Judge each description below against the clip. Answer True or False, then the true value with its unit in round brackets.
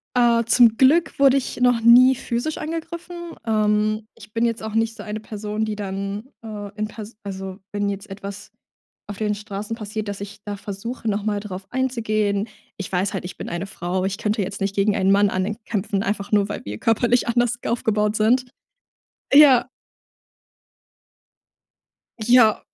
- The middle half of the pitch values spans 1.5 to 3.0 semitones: True (2.6 semitones)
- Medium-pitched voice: False (215 Hz)